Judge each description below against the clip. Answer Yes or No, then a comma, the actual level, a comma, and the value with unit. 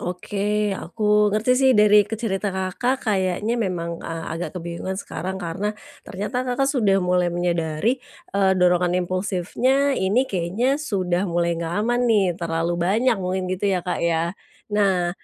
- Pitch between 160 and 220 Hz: Yes, high, 190 Hz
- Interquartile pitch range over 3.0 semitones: Yes, average, 3.5 semitones